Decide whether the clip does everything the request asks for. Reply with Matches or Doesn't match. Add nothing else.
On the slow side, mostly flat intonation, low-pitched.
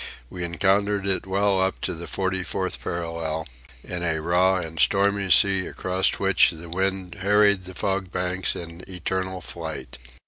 Doesn't match